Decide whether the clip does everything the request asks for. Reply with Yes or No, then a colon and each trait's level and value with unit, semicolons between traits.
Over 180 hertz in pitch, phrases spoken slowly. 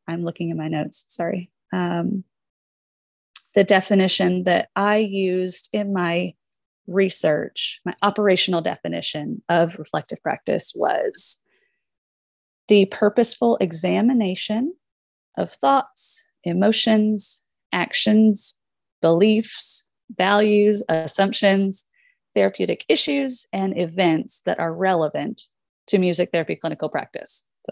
Yes: high, 190 Hz; slow, 95 wpm